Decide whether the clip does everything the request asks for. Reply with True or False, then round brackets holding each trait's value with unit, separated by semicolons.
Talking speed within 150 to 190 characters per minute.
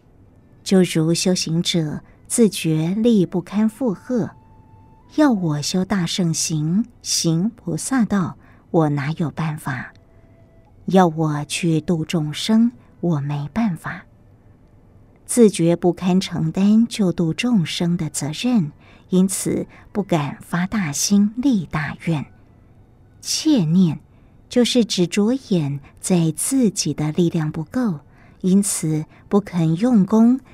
True (160 characters per minute)